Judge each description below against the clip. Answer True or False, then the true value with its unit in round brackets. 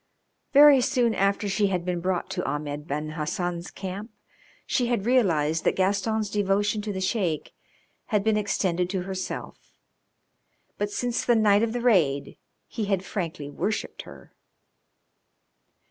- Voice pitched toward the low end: False (195 Hz)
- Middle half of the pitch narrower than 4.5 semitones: True (3.7 semitones)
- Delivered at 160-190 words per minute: False (145 wpm)